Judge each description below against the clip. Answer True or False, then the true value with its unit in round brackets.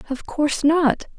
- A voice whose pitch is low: False (295 Hz)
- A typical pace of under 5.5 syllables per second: True (4.6 syllables/s)